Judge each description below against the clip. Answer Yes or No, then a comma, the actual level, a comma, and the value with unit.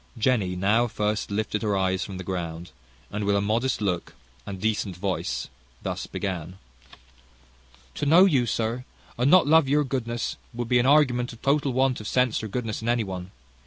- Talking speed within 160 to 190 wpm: Yes, average, 180 wpm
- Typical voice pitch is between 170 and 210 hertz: No, low, 110 Hz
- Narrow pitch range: No, average, 4.7 semitones